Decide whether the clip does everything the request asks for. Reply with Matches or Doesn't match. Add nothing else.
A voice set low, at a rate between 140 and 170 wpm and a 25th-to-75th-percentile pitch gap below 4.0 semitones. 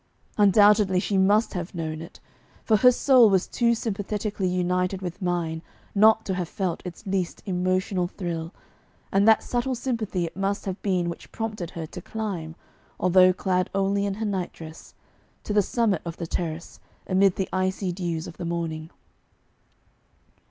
Doesn't match